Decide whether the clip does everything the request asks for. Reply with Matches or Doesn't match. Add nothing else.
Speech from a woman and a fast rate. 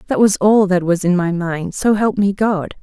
Matches